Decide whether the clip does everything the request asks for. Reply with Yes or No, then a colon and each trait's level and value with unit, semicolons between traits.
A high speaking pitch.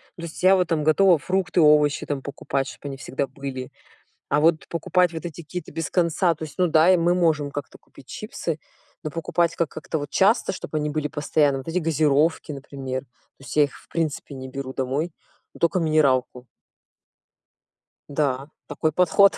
No: medium, 155 Hz